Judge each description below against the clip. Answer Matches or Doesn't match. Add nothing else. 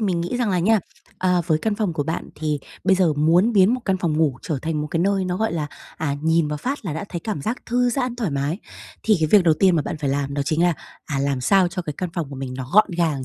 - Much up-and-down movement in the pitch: Doesn't match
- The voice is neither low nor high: Matches